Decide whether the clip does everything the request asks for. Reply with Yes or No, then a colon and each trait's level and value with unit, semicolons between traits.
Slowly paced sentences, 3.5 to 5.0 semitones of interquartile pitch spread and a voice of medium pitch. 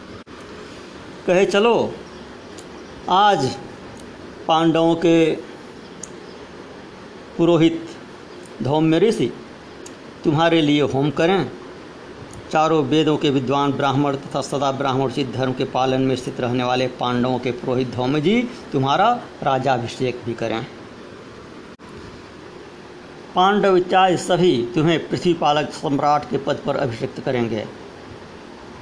Yes: slow, 100 wpm; average, 3.9 semitones; medium, 145 Hz